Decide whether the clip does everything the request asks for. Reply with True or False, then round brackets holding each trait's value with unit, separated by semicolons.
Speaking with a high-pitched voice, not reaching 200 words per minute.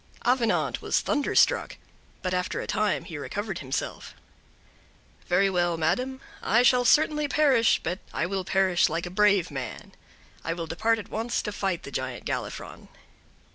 True (195 Hz; 155 wpm)